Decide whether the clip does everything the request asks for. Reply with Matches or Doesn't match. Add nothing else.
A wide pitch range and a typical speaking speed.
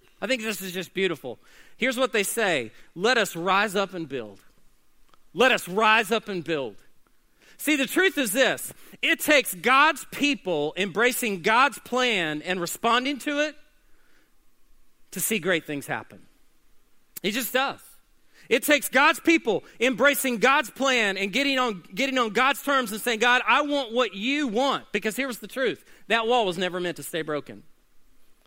Matches